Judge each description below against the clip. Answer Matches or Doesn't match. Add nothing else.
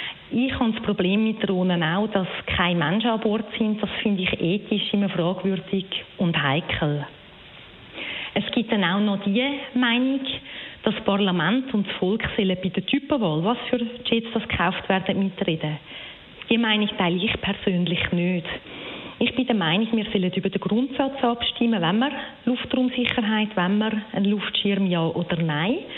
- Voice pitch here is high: Matches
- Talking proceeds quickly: Doesn't match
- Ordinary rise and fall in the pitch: Matches